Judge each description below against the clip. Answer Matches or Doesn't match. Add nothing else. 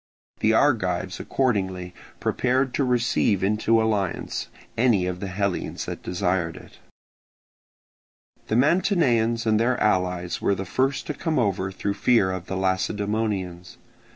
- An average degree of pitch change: Matches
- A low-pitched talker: Matches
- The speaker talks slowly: Matches